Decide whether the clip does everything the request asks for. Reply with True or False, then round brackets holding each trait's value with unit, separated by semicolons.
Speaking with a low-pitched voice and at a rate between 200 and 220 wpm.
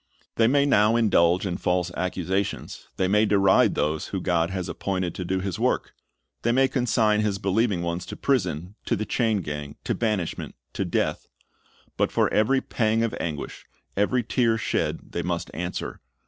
False (100 Hz; 175 wpm)